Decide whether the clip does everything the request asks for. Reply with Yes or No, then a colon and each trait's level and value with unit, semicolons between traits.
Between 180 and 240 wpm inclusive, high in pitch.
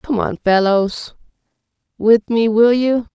No: slow, 135 wpm; high, 220 Hz